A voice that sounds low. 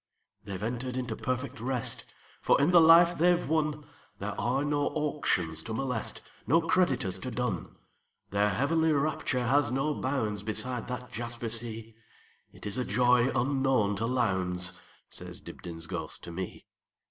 Yes: low, 125 Hz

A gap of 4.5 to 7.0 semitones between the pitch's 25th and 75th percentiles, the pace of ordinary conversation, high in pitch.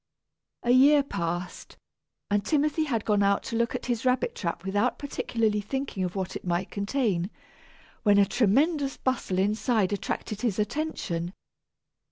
Yes: average, 5.0 semitones; average, 150 wpm; high, 215 Hz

